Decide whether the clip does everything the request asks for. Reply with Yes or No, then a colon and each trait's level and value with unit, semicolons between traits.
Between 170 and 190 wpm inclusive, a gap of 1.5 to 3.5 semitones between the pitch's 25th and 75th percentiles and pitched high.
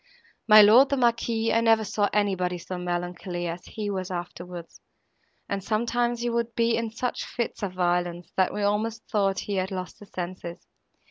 No: average, 180 wpm; average, 4.2 semitones; high, 205 Hz